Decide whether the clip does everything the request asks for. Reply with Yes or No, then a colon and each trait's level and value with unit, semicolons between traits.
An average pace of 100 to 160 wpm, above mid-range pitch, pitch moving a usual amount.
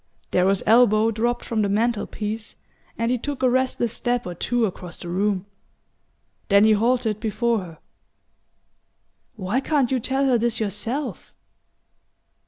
Yes: average, 145 wpm; high, 225 Hz; average, 3.0 semitones